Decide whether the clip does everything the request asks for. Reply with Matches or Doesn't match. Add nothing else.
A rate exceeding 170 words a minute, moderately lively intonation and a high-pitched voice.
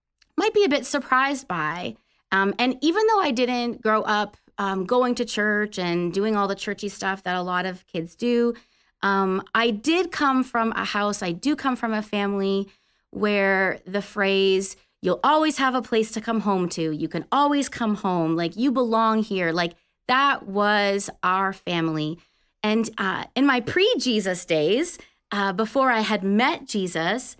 Matches